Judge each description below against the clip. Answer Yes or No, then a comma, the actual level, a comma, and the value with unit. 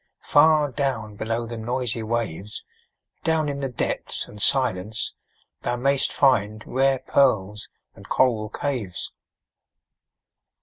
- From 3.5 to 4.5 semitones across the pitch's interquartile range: Yes, average, 4.1 semitones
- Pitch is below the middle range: Yes, low, 120 Hz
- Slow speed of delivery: Yes, slow, 115 wpm